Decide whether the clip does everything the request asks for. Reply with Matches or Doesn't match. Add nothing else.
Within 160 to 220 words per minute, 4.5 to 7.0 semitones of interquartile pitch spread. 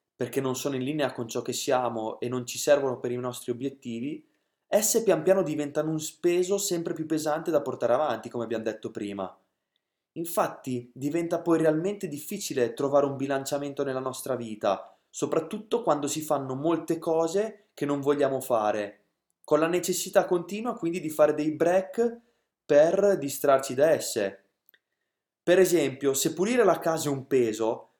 Matches